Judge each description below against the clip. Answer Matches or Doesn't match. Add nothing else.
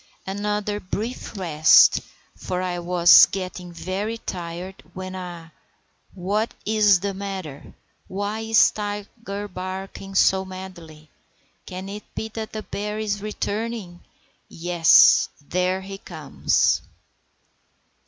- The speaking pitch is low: Doesn't match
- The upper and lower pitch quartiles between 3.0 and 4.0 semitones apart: Doesn't match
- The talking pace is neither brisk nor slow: Doesn't match